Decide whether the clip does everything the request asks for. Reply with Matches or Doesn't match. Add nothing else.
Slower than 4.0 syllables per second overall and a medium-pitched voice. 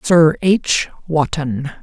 Matches